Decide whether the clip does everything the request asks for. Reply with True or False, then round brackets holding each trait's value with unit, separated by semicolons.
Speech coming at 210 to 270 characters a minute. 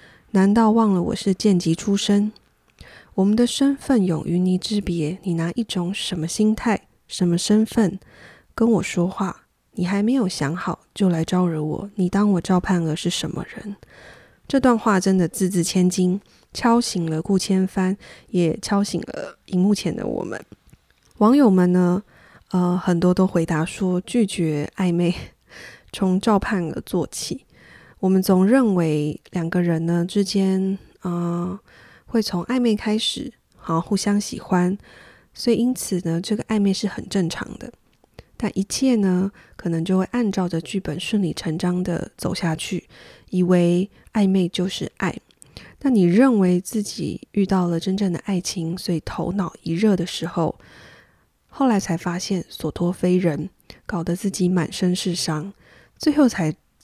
True (225 characters per minute)